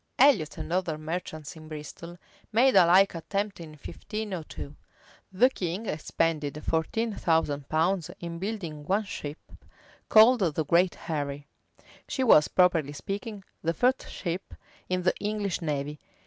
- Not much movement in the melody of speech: No, average, 4.3 semitones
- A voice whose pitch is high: No, medium, 170 Hz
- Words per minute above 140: No, slow, 135 wpm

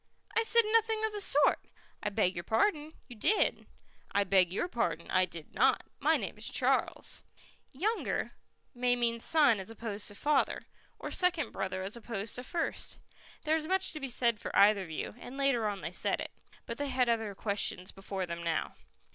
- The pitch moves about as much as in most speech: No, wide, 7.5 semitones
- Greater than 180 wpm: Yes, average, 190 wpm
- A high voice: Yes, high, 235 Hz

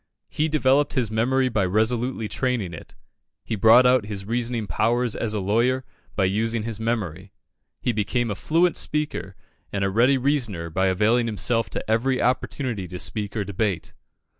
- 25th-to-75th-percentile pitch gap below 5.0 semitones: Yes, average, 3.7 semitones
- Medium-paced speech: Yes, average, 165 wpm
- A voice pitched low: Yes, low, 115 Hz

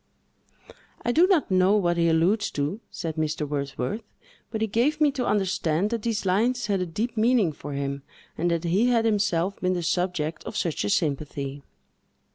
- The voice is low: No, medium, 185 Hz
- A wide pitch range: Yes, wide, 5.7 semitones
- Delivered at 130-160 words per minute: No, average, 185 wpm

